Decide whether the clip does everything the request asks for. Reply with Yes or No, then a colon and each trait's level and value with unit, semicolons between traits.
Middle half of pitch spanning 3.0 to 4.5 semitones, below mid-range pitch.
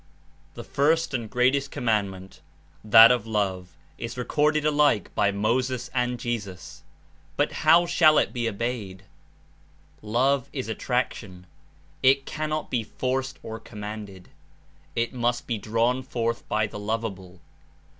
Yes: average, 3.8 semitones; low, 120 Hz